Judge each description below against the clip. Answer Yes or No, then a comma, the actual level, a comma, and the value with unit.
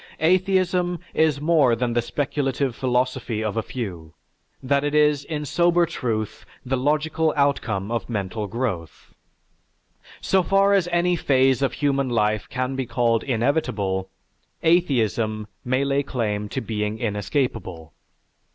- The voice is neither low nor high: No, low, 130 Hz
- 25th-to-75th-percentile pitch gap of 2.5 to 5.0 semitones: No, wide, 5.4 semitones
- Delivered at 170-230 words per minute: No, slow, 135 wpm